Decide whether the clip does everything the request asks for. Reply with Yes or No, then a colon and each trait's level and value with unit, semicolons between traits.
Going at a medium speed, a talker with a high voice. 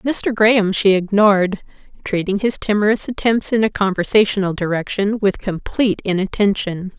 No: slow, 130 wpm; high, 200 Hz